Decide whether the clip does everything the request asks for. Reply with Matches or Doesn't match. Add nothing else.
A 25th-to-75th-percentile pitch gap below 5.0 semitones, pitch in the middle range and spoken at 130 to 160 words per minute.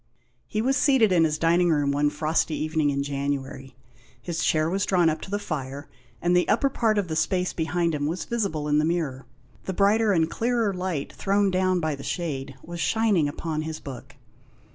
Doesn't match